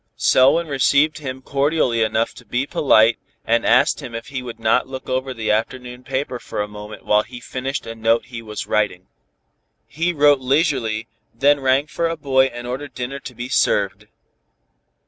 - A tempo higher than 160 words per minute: Yes, average, 180 wpm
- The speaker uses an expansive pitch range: No, average, 3.4 semitones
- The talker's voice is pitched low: Yes, low, 130 Hz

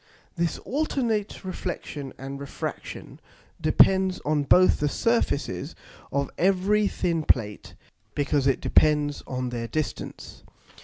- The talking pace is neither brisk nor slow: No, slow, 110 wpm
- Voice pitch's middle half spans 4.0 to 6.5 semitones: Yes, average, 5.2 semitones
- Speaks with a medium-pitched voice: Yes, medium, 155 Hz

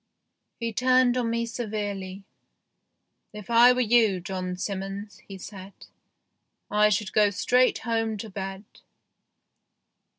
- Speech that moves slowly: Yes, slow, 130 wpm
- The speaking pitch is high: Yes, high, 210 Hz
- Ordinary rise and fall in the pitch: Yes, average, 3.2 semitones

